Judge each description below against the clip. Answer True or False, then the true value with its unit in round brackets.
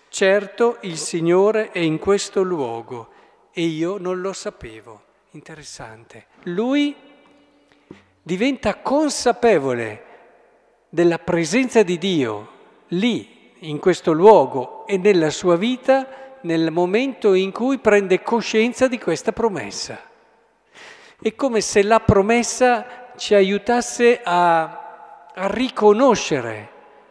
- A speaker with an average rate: False (105 wpm)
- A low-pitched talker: False (205 Hz)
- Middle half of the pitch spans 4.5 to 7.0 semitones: True (5.5 semitones)